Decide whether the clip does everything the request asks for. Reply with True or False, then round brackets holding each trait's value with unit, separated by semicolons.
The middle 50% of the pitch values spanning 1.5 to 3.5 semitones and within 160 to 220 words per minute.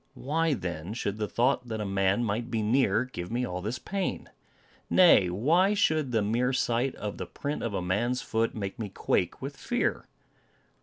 False (4.2 semitones; 190 wpm)